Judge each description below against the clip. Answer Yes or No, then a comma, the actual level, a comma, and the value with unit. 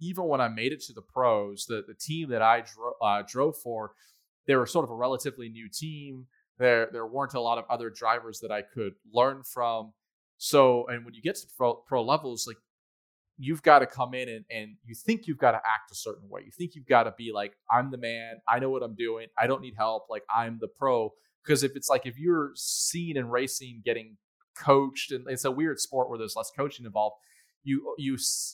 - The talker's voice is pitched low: Yes, low, 125 Hz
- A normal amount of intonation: Yes, average, 3.5 semitones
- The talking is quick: Yes, fast, 230 wpm